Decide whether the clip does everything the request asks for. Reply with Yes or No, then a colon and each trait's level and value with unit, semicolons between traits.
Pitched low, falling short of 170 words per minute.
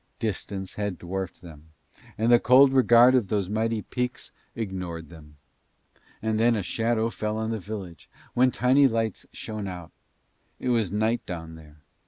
Yes: low, 110 Hz; average, 160 wpm